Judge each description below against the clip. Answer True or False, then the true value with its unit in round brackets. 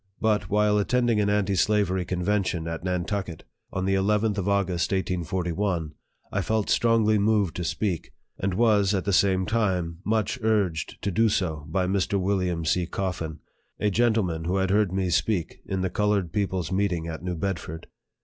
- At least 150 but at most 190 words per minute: True (170 wpm)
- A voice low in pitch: True (95 Hz)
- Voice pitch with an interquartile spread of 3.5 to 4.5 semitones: False (2.7 semitones)